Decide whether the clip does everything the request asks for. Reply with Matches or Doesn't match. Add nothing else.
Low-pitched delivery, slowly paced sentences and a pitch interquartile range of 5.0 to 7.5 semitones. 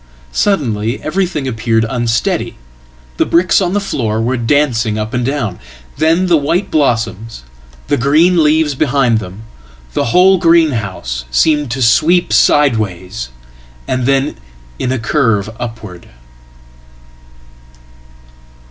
Matches